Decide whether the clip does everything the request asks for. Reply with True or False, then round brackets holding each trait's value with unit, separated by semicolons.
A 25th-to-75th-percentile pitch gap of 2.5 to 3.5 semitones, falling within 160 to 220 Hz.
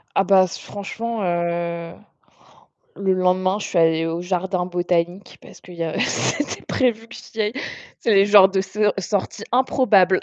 True (2.9 semitones; 190 Hz)